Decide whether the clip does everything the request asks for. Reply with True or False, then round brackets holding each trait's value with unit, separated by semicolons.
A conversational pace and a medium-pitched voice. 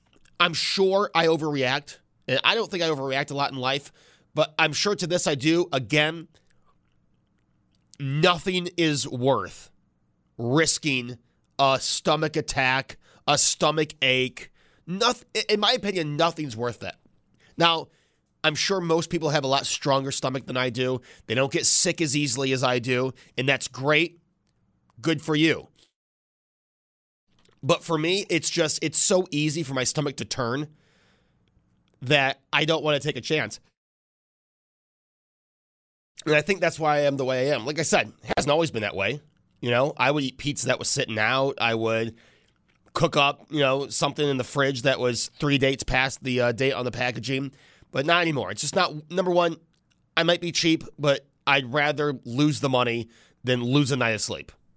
True (180 wpm; 145 Hz)